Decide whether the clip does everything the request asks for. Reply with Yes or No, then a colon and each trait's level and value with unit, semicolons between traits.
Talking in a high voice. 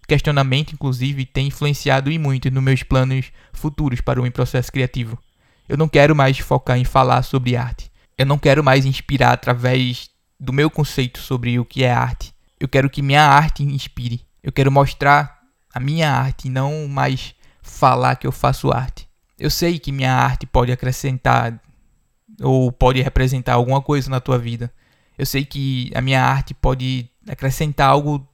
No: low, 135 Hz